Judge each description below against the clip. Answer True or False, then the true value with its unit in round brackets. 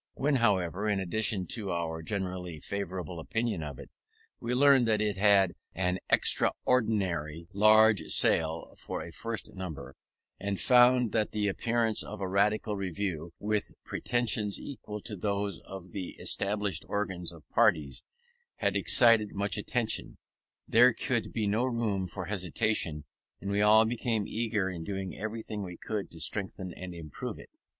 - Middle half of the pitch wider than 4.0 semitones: False (3.3 semitones)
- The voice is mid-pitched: False (100 Hz)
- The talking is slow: False (150 wpm)